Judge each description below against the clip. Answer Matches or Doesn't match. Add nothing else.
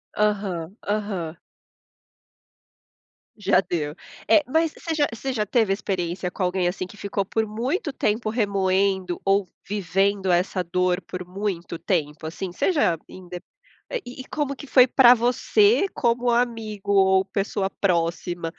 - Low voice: Doesn't match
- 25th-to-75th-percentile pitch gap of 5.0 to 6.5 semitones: Doesn't match